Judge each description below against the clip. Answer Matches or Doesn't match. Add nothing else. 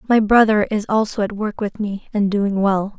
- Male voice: Doesn't match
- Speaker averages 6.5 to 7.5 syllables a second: Doesn't match